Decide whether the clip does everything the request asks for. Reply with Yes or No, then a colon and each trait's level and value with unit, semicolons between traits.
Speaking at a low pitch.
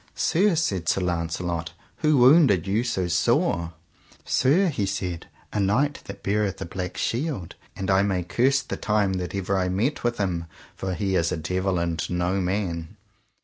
Yes: very low, 95 Hz